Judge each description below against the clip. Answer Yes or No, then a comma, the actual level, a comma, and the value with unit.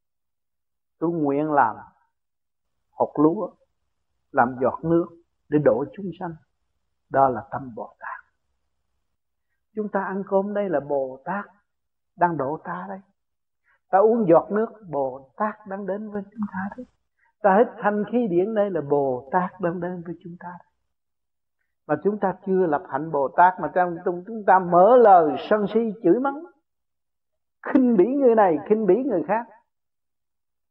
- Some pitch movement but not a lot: No, wide, 7.5 semitones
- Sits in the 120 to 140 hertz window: No, medium, 175 Hz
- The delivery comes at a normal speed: No, slow, 160 wpm